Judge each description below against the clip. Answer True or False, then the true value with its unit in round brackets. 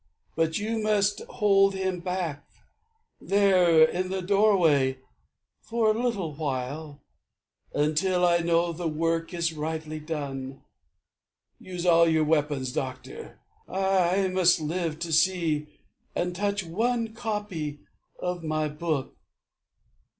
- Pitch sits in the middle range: True (170 Hz)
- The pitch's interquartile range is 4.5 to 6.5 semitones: False (3.7 semitones)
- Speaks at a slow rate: True (115 wpm)